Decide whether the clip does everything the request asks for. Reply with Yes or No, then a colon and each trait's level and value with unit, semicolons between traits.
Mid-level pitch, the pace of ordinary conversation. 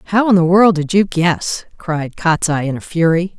No: medium, 170 Hz; fast, 215 wpm